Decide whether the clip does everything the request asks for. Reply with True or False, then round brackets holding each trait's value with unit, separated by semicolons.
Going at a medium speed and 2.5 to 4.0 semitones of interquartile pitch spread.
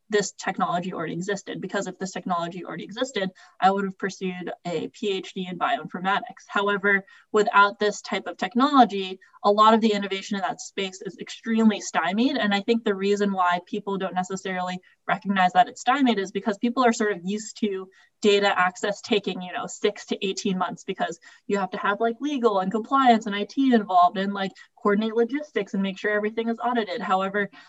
True (190 wpm; 2.9 semitones)